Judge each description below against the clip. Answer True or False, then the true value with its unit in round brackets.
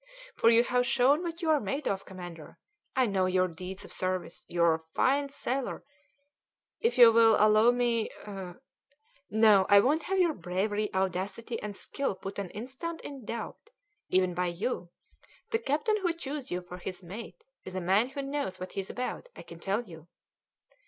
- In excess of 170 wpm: True (185 wpm)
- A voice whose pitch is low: False (220 Hz)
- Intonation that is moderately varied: False (6.7 semitones)